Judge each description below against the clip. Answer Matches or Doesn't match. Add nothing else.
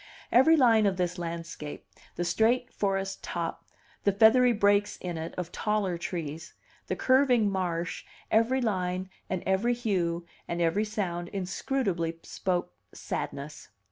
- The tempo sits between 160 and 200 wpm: Doesn't match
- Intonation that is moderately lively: Matches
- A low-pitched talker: Doesn't match